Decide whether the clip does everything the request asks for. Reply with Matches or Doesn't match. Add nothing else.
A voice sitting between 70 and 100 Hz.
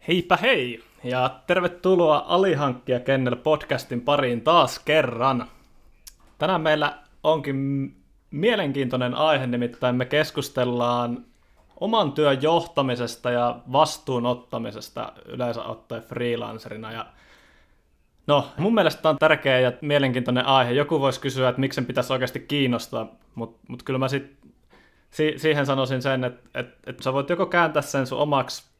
Doesn't match